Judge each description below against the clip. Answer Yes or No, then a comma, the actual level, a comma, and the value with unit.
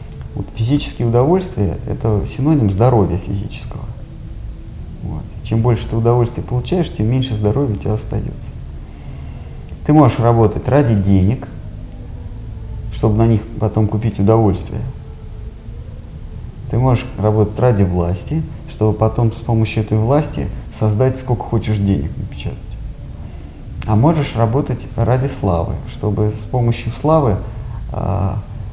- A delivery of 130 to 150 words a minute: No, average, 115 wpm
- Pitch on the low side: Yes, low, 110 Hz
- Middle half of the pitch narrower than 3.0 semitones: Yes, narrow, 2.6 semitones